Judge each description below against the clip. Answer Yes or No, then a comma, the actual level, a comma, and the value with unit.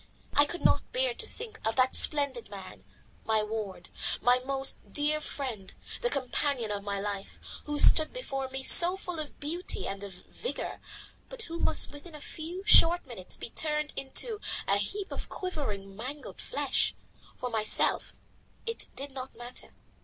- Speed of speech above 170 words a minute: No, average, 165 wpm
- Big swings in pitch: Yes, wide, 7.1 semitones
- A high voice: Yes, very high, 275 Hz